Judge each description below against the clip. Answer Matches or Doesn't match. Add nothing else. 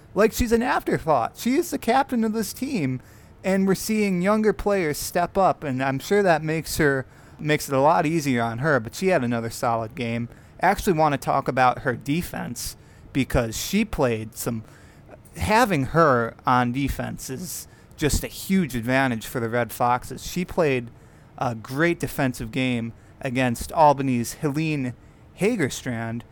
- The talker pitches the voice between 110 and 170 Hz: Matches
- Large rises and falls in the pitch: Matches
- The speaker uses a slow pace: Doesn't match